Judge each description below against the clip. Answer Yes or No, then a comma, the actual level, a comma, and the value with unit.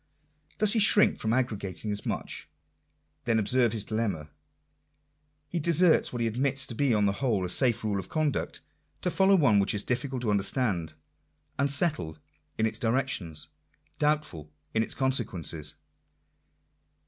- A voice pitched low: Yes, low, 115 Hz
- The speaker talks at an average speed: Yes, average, 150 wpm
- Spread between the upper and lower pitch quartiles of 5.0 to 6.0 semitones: Yes, wide, 5.6 semitones